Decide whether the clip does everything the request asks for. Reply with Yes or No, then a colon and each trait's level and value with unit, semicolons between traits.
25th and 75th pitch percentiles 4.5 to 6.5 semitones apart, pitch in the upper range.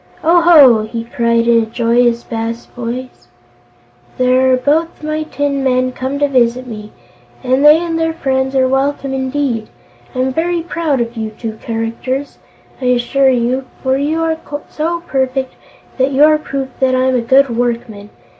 No: average, 3.3 semitones; very high, 260 Hz